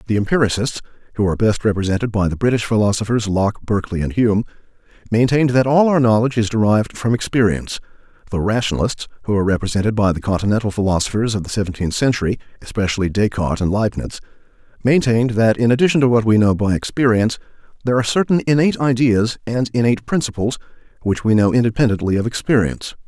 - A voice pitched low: Yes, low, 110 Hz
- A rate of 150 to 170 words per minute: Yes, average, 155 wpm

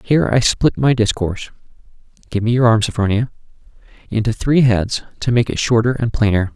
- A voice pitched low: Yes, low, 115 Hz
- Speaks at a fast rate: No, average, 175 wpm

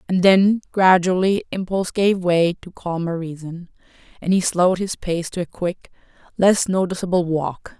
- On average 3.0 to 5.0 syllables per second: Yes, 4.7 syllables/s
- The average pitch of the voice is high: No, medium, 180 Hz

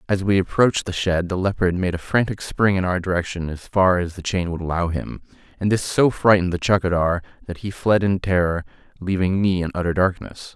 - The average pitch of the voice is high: No, very low, 90 Hz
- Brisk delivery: Yes, fast, 215 wpm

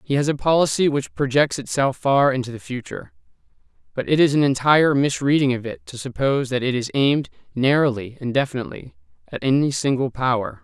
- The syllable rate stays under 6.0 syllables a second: No, 6.1 syllables/s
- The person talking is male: Yes, male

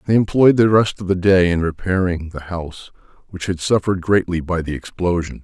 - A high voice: No, very low, 90 Hz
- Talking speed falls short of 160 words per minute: No, average, 200 wpm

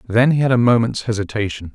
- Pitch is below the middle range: Yes, low, 115 Hz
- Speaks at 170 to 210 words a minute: Yes, fast, 205 wpm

